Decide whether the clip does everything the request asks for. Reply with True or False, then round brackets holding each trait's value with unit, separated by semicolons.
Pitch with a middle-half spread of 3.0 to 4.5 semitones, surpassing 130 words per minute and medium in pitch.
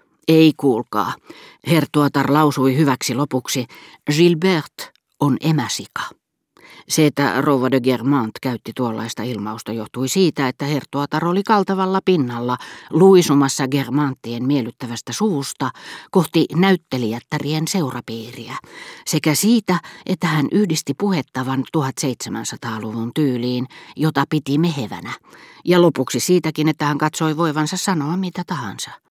False (4.2 semitones; 105 wpm; 145 Hz)